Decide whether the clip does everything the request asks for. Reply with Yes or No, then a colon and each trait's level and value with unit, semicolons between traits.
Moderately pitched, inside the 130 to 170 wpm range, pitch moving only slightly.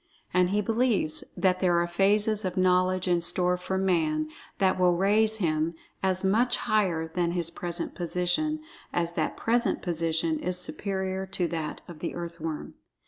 Yes: medium, 180 Hz; average, 160 wpm; narrow, 2.1 semitones